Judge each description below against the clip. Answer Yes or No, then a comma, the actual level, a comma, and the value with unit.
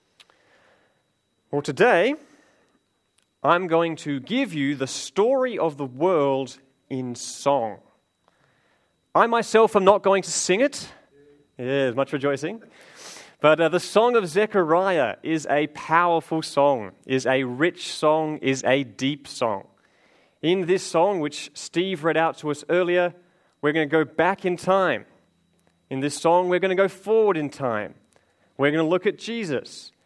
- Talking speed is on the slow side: No, average, 155 wpm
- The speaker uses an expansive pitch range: No, average, 4.9 semitones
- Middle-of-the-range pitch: Yes, medium, 160 Hz